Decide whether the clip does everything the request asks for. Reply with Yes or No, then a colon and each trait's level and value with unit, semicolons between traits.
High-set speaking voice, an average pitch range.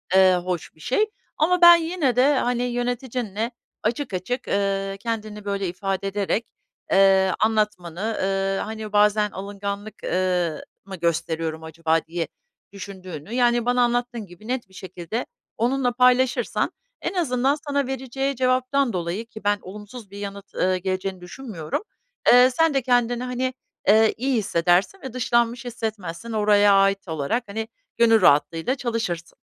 Yes: high, 215 Hz; average, 4.5 semitones